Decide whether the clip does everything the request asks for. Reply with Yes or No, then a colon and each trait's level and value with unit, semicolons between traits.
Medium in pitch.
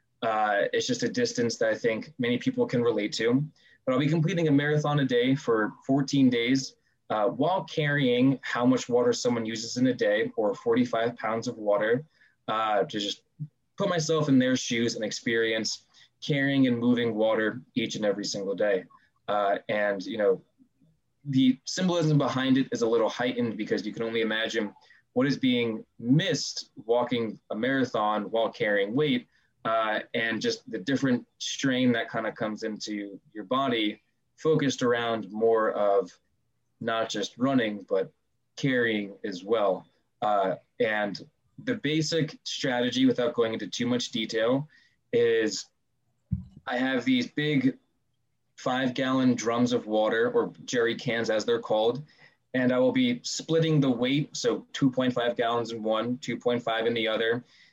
No: low, 125 Hz